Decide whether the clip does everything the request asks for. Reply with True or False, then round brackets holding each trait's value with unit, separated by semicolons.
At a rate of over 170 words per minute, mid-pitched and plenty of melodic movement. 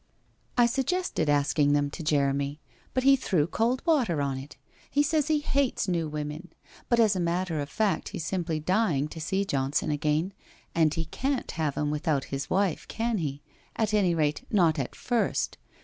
True (185 wpm; 165 Hz; 7.1 semitones)